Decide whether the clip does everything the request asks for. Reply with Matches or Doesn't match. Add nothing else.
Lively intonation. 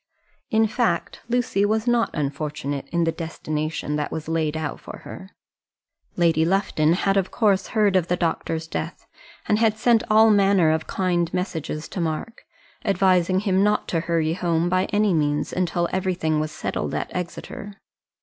Doesn't match